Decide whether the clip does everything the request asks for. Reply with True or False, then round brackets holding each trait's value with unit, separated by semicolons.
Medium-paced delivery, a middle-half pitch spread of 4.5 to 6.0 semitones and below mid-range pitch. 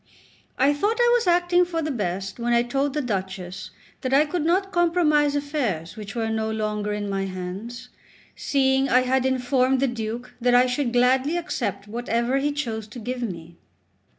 False (180 wpm; 5.1 semitones; 250 Hz)